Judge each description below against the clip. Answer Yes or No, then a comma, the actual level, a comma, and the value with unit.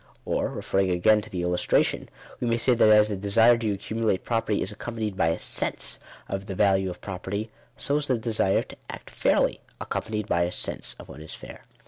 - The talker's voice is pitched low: Yes, low, 105 Hz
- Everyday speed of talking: No, fast, 210 wpm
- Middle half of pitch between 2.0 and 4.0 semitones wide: Yes, average, 2.9 semitones